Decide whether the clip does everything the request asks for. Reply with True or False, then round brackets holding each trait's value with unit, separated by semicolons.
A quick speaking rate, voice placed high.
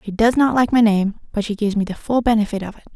True (305 wpm; 215 Hz)